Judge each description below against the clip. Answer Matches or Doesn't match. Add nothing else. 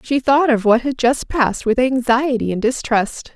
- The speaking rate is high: Doesn't match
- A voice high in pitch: Matches